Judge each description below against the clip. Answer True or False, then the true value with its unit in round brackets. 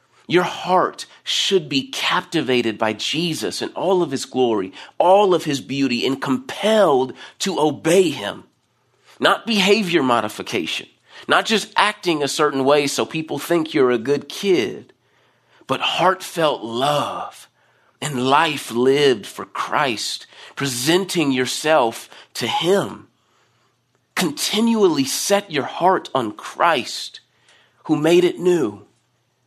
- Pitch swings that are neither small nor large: False (6.1 semitones)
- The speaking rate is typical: False (120 wpm)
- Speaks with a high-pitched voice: False (155 Hz)